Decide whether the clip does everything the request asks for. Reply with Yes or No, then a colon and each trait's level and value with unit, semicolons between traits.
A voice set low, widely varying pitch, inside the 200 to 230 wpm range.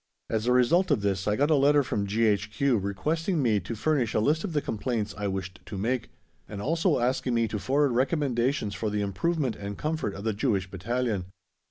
Yes: low, 115 Hz; wide, 5.8 semitones; fast, 205 wpm